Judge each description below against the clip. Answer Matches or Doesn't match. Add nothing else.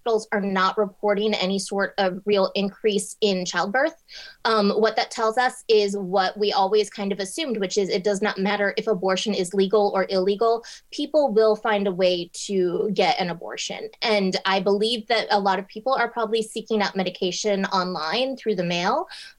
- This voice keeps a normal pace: Matches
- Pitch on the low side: Doesn't match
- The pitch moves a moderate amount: Doesn't match